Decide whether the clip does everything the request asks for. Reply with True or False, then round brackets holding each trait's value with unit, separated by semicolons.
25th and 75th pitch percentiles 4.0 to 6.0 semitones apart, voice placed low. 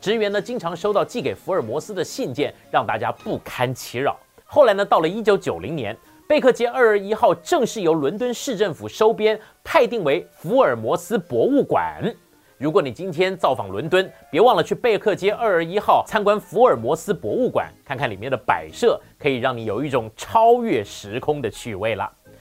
False (5.2 semitones; 210 Hz)